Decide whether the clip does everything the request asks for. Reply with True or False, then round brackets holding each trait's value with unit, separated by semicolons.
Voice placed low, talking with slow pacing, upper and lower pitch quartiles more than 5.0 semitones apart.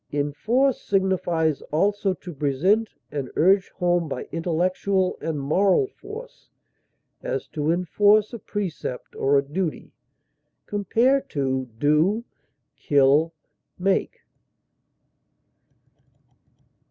False (180 Hz; 90 wpm; 5.5 semitones)